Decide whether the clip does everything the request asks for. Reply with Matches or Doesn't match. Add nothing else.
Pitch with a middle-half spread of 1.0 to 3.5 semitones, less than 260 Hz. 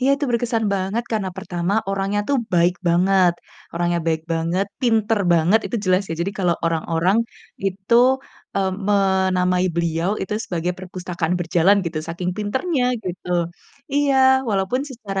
Matches